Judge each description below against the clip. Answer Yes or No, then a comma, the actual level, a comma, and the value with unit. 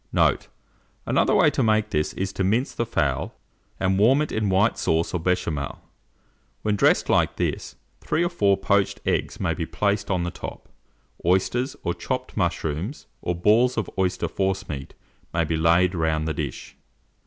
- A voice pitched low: Yes, very low, 95 Hz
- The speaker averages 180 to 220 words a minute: No, average, 170 wpm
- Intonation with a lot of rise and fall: No, average, 4.3 semitones